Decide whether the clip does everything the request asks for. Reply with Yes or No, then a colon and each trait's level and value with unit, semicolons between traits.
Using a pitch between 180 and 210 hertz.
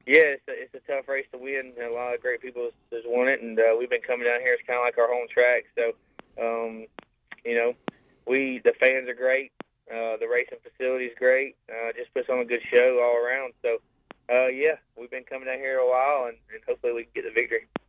No: low, 130 Hz